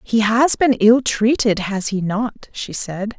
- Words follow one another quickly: No, average, 190 wpm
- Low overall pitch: No, high, 220 Hz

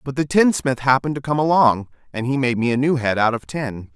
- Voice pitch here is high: No, low, 135 Hz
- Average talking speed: No, fast, 260 wpm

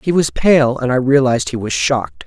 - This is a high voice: No, low, 125 Hz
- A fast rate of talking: Yes, fast, 240 wpm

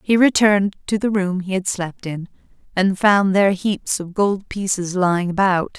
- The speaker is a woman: Yes, female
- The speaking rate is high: No, average, 185 wpm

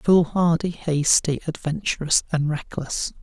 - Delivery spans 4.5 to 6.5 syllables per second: No, 4.0 syllables/s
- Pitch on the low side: No, medium, 160 Hz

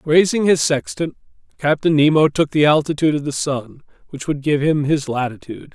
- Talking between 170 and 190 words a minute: Yes, average, 180 wpm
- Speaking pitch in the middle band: Yes, medium, 150 Hz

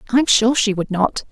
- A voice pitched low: No, high, 225 Hz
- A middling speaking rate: No, fast, 230 wpm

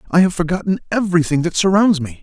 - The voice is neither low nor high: Yes, medium, 175 Hz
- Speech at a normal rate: Yes, average, 190 wpm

